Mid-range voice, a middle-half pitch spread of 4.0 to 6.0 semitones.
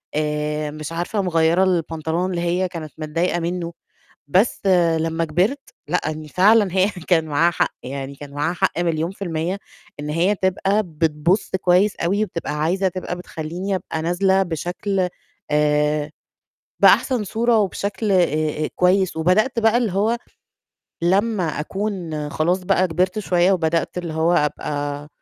No: medium, 175 Hz; average, 3.5 semitones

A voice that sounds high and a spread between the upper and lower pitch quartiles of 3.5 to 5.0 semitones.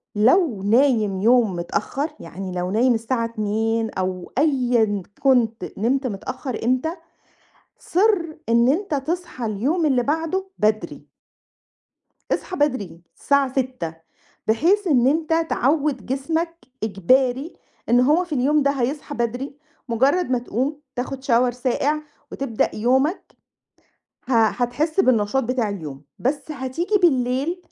Yes: very high, 255 Hz; average, 4.7 semitones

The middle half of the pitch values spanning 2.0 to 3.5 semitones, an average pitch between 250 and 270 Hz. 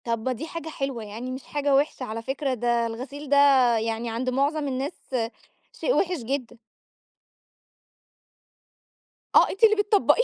No: average, 4.0 semitones; very high, 265 Hz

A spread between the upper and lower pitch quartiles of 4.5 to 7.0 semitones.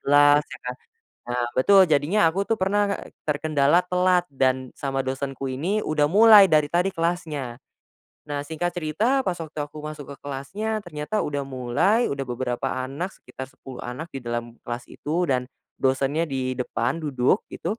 Yes: average, 5.0 semitones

